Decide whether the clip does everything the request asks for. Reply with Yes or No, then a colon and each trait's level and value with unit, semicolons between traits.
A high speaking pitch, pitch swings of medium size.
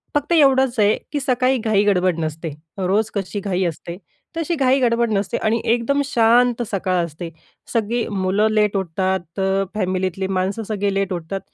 Yes: high, 205 Hz; average, 4.1 semitones